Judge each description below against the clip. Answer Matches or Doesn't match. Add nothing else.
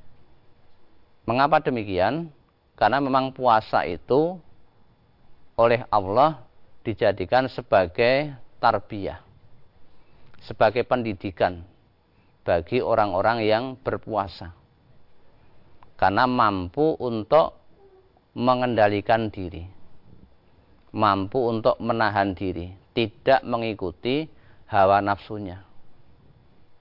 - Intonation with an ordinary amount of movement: Matches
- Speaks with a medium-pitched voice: Doesn't match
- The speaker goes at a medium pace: Doesn't match